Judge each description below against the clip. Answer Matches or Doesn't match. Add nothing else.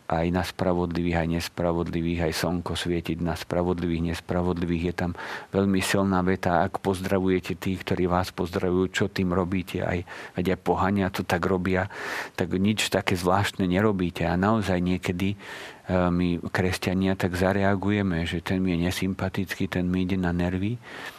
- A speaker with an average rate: Matches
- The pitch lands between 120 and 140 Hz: Doesn't match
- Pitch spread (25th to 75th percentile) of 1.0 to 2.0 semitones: Matches